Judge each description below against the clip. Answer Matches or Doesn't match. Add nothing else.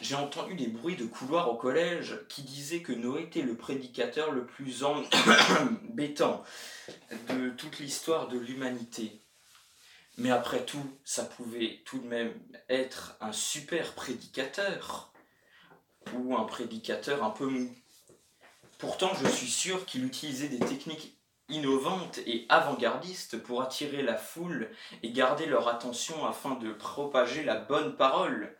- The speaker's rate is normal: Doesn't match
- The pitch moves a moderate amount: Matches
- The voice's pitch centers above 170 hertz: Doesn't match